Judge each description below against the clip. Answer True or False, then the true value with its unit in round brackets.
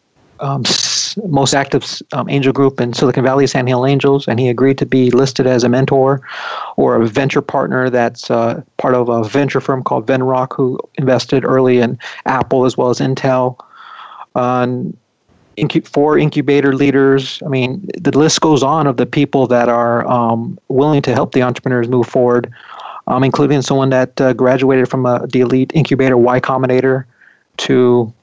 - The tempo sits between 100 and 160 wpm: False (175 wpm)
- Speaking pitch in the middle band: False (130 Hz)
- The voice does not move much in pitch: True (1.7 semitones)